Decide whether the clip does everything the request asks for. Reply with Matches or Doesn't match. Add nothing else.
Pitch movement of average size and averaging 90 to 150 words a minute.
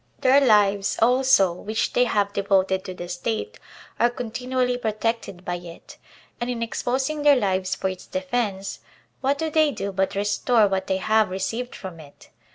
Doesn't match